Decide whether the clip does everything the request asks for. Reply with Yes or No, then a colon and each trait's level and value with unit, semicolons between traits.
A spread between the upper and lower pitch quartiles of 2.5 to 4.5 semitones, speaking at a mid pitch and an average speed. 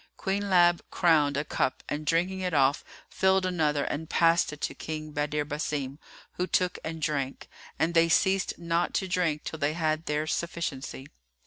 Yes: average, 2.8 semitones; medium, 160 Hz; average, 180 wpm